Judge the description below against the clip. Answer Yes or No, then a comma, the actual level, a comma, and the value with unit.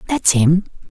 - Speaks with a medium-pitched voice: Yes, medium, 180 Hz